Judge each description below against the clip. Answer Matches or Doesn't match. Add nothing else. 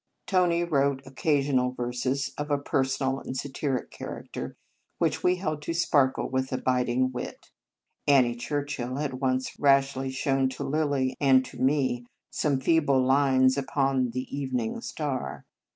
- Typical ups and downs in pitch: Doesn't match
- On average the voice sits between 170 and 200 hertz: Doesn't match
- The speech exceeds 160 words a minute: Doesn't match